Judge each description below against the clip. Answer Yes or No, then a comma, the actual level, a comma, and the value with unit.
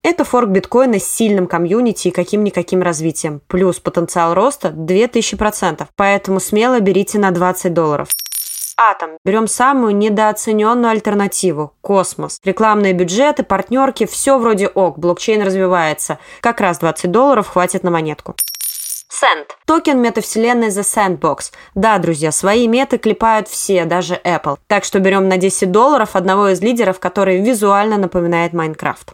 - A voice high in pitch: Yes, high, 195 Hz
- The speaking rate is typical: Yes, average, 135 wpm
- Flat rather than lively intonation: No, average, 3.6 semitones